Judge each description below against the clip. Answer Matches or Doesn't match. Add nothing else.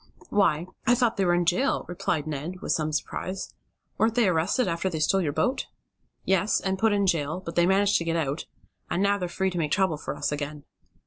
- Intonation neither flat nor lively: Matches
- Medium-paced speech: Doesn't match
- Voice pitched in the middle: Matches